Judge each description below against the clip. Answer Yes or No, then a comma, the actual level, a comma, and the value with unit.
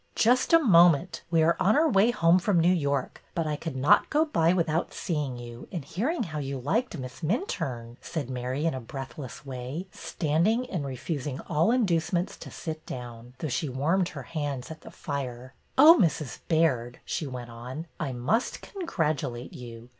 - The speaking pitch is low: No, medium, 155 Hz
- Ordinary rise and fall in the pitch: No, wide, 5.7 semitones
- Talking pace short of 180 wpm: No, average, 190 wpm